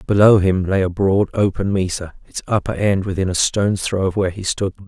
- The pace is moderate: No, fast, 220 wpm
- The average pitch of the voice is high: No, very low, 95 Hz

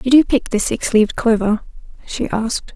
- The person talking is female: Yes, female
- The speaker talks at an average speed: Yes, average, 195 wpm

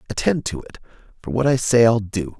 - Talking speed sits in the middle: No, fast, 225 wpm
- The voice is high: No, low, 110 Hz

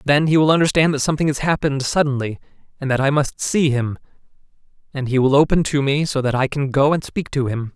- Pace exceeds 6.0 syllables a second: Yes, 6.2 syllables/s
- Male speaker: Yes, male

